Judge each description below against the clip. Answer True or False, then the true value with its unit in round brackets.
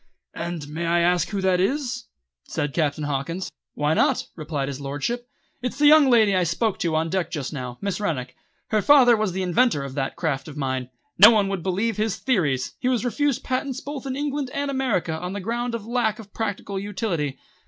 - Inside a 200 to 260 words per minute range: True (205 wpm)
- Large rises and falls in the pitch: True (7.3 semitones)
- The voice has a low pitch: False (190 Hz)